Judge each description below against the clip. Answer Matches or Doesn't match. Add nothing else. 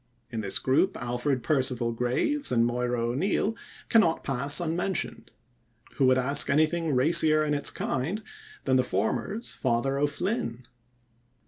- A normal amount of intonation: Matches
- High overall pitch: Doesn't match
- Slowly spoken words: Matches